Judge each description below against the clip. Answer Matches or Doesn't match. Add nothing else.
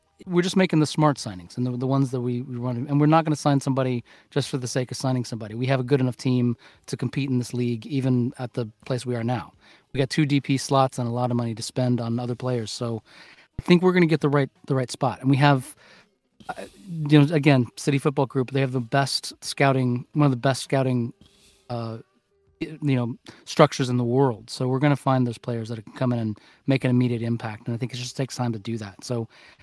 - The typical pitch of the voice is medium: Doesn't match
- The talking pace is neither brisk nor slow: Doesn't match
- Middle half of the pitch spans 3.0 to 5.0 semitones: Doesn't match